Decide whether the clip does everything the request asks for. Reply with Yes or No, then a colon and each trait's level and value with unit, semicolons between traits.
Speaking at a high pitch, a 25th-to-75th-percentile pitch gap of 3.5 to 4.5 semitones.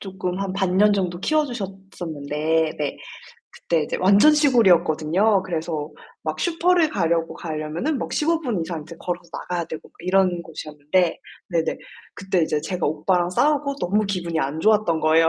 No: medium, 180 Hz; average, 4.1 semitones